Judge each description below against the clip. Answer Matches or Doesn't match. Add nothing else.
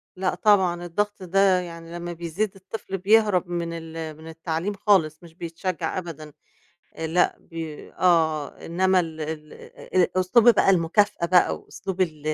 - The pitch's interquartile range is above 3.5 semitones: Doesn't match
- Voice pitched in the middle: Matches